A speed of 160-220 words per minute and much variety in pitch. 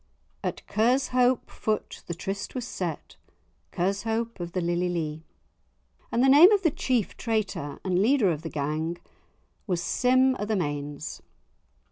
No: average, 145 wpm; wide, 6.4 semitones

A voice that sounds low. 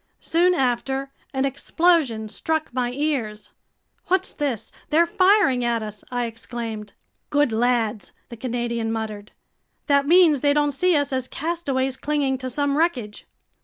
No: very high, 265 Hz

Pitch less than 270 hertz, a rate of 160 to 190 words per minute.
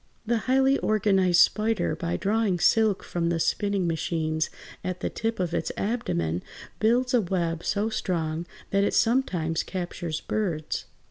No: high, 190 Hz; average, 145 wpm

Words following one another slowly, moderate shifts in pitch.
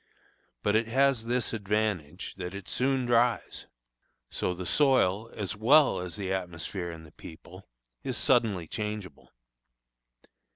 Yes: slow, 130 wpm; average, 4.8 semitones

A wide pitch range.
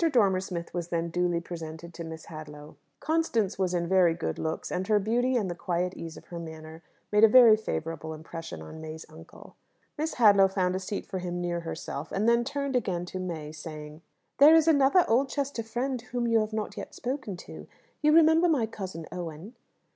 Yes: wide, 6.2 semitones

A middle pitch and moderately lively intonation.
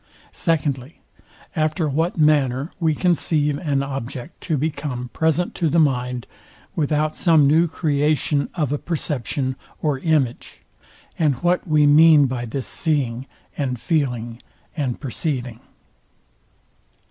Yes: medium, 145 Hz; average, 3.3 semitones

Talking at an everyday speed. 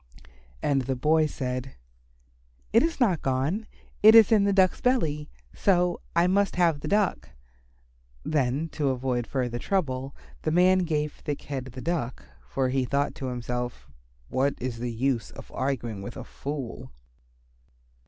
Yes: average, 155 wpm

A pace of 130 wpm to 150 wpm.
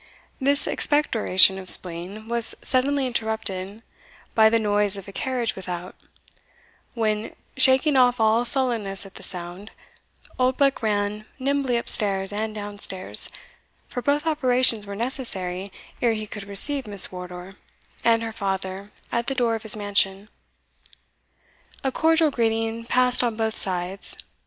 Yes: average, 140 wpm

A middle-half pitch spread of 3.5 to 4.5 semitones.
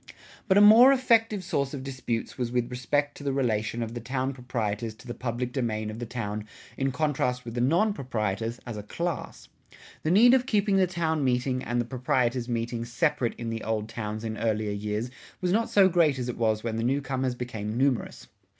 Yes: average, 4.1 semitones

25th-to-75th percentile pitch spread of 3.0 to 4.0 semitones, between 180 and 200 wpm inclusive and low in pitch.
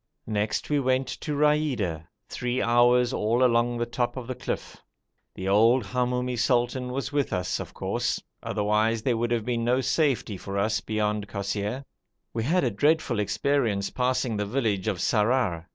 No: average, 3.5 semitones; average, 170 wpm; low, 120 Hz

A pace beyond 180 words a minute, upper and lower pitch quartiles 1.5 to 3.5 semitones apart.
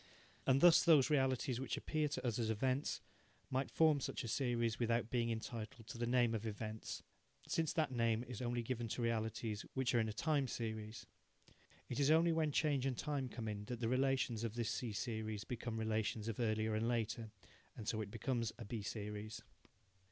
Yes: average, 195 wpm; average, 3.0 semitones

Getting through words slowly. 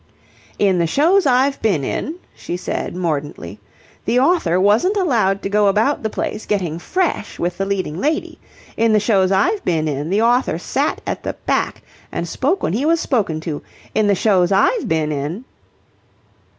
No: average, 175 wpm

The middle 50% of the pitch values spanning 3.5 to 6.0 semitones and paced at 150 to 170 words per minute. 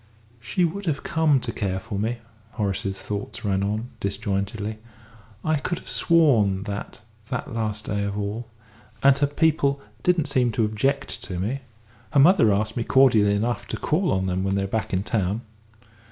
No: wide, 5.5 semitones; average, 180 wpm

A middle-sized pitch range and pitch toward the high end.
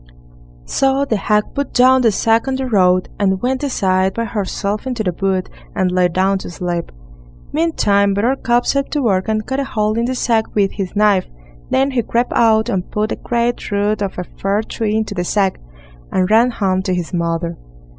Yes: average, 4.2 semitones; high, 210 Hz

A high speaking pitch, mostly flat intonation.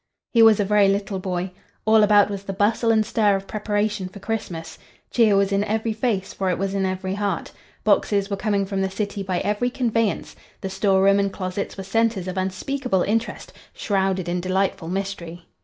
Yes: high, 200 Hz; narrow, 1.9 semitones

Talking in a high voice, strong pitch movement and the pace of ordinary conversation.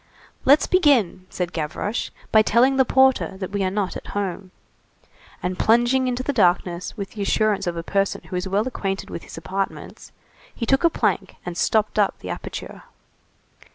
No: high, 200 Hz; average, 4.7 semitones; average, 180 wpm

